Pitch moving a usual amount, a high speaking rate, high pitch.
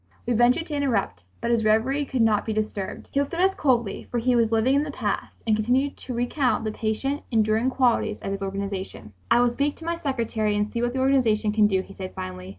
Yes: average, 3.9 semitones; fast, 240 wpm; high, 230 Hz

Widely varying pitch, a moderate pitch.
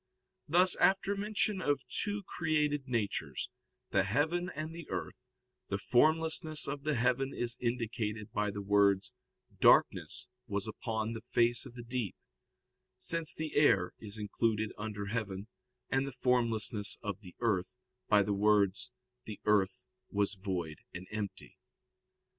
No: wide, 6.0 semitones; low, 115 Hz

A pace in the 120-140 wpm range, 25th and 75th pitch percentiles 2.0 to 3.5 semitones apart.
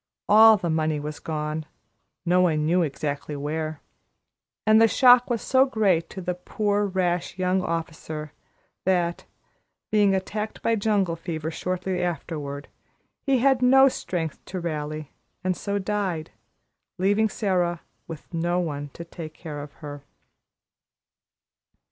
No: slow, 135 wpm; average, 4.5 semitones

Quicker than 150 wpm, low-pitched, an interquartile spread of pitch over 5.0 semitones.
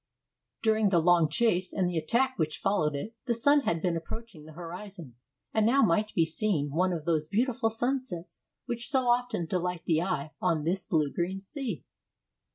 No: average, 180 wpm; medium, 185 Hz; wide, 5.6 semitones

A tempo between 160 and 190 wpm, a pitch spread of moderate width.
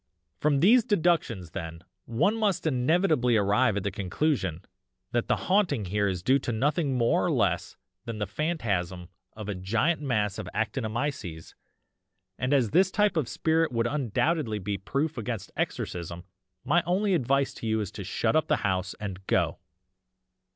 No: average, 165 wpm; wide, 7.8 semitones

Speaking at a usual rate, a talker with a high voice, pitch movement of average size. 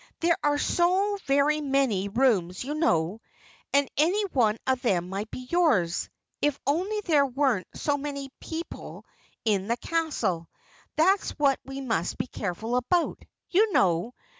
No: average, 150 wpm; very high, 275 Hz; wide, 6.7 semitones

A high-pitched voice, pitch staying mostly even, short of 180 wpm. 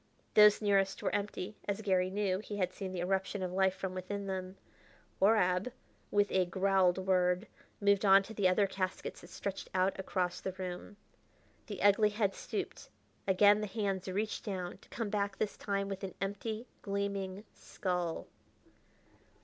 Yes: high, 195 Hz; narrow, 1.7 semitones; average, 165 wpm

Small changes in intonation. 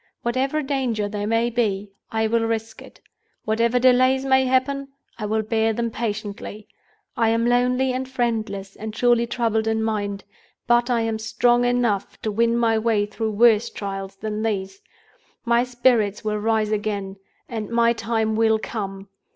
Yes: narrow, 2.1 semitones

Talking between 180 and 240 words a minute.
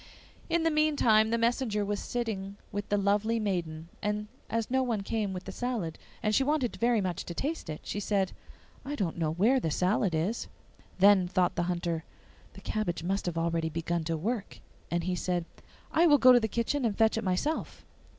Yes: average, 200 wpm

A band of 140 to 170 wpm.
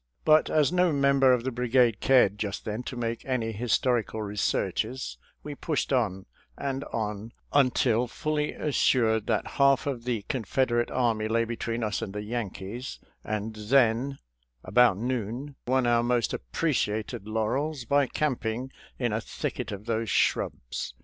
Yes: average, 155 wpm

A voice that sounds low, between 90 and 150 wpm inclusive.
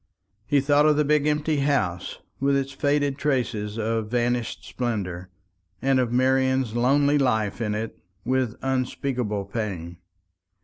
Yes: low, 130 Hz; slow, 135 wpm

